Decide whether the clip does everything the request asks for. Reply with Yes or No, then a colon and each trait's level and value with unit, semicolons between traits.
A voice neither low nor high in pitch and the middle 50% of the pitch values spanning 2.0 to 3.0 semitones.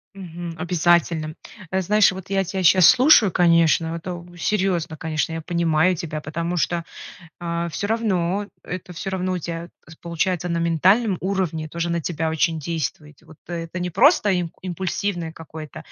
Yes: medium, 170 Hz; narrow, 2.4 semitones